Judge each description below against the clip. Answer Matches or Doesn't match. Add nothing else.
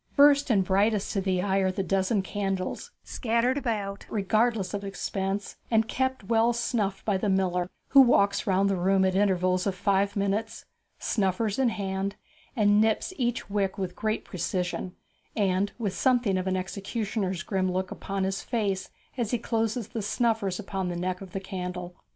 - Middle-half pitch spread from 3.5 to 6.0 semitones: Doesn't match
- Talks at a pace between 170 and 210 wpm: Matches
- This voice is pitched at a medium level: Doesn't match